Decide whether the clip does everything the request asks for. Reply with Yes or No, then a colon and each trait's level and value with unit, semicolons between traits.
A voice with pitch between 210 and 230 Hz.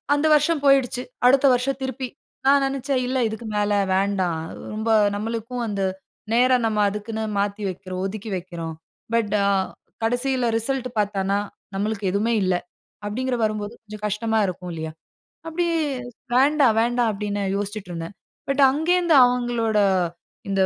Yes: high, 225 Hz